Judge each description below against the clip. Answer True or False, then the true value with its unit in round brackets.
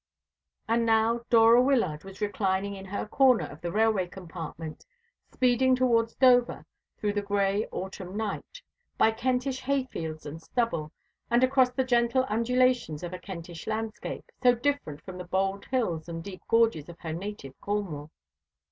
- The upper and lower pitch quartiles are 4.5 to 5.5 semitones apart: True (5.2 semitones)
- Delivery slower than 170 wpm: True (155 wpm)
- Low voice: False (210 Hz)